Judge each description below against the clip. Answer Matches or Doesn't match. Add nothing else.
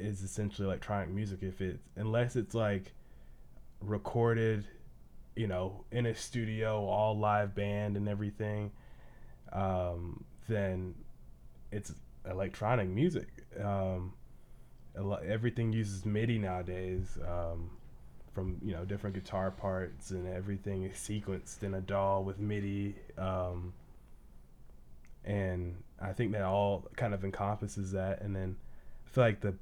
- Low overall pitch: Matches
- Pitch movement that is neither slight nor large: Doesn't match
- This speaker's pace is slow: Matches